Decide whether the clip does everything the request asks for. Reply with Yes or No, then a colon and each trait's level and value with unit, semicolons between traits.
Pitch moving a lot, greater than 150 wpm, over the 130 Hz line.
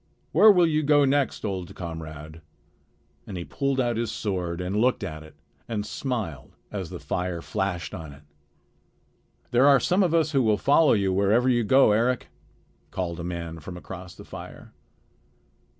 No: wide, 7.4 semitones; average, 170 wpm; low, 105 Hz